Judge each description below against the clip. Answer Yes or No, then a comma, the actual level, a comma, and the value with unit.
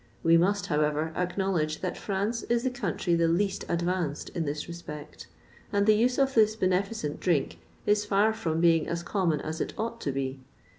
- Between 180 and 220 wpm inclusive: Yes, average, 185 wpm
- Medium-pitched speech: Yes, medium, 180 Hz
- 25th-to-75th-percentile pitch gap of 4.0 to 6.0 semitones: Yes, average, 4.5 semitones